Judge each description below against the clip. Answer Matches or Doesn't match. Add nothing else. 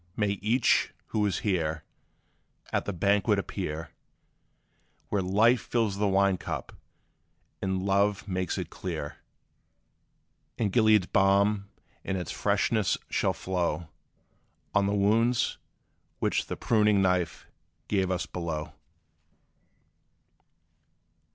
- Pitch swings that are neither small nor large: Doesn't match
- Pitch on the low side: Matches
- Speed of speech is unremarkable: Doesn't match